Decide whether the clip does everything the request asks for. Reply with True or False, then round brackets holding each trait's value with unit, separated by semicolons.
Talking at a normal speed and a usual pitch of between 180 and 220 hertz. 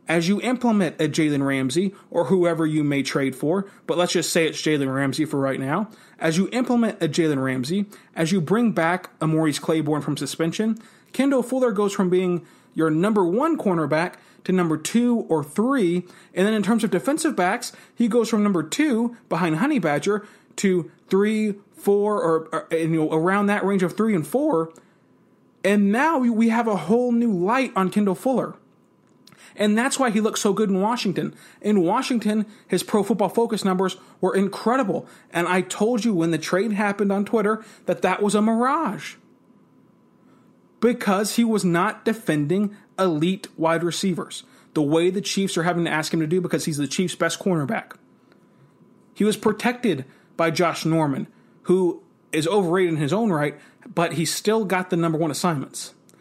True (180 wpm; 190 Hz)